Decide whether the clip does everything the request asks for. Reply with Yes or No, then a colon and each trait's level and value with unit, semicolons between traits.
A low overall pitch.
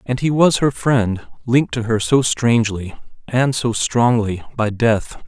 Yes: low, 120 Hz